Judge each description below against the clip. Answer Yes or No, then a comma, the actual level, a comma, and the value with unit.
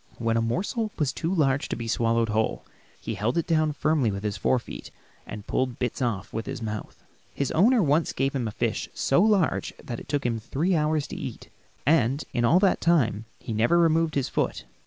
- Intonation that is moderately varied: No, wide, 5.9 semitones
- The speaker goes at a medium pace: No, fast, 220 wpm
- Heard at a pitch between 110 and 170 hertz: Yes, low, 135 Hz